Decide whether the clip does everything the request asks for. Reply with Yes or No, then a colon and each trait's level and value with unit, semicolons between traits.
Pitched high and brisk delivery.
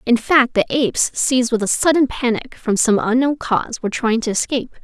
Yes: high, 240 Hz; fast, 210 wpm